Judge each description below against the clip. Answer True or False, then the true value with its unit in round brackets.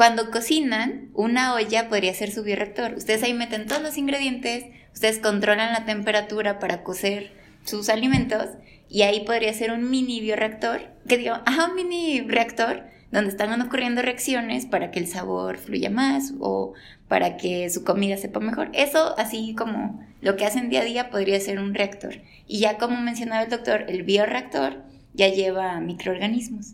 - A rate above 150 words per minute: True (170 wpm)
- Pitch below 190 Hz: False (220 Hz)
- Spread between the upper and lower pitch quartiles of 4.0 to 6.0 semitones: False (3.2 semitones)